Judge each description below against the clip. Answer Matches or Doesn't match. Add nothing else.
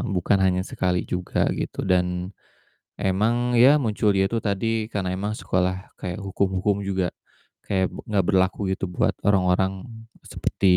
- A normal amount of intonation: Doesn't match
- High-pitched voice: Doesn't match